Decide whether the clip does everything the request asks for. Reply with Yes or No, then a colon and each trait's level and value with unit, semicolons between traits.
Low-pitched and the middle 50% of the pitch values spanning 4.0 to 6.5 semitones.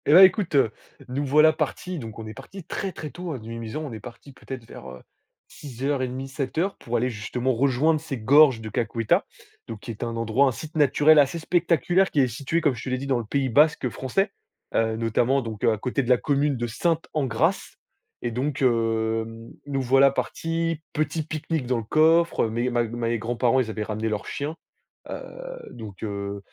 Yes: low, 130 Hz; average, 4.9 semitones